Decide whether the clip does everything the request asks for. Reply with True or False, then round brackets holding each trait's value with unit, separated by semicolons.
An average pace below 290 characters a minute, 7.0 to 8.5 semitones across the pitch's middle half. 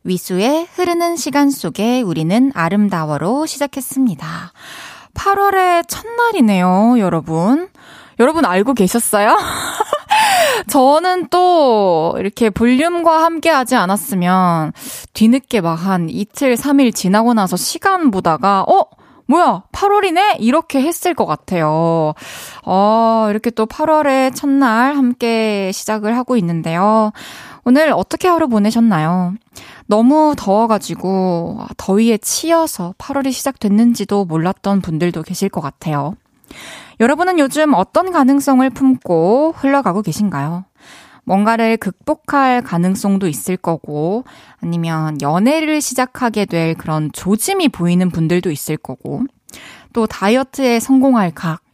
True (270 characters per minute; 7.7 semitones)